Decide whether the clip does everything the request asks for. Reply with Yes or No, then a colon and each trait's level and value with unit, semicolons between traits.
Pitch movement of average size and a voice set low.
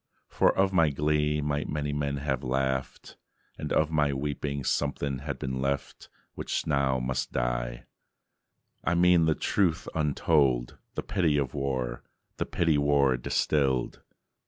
No: narrow, 2.3 semitones; very low, 70 Hz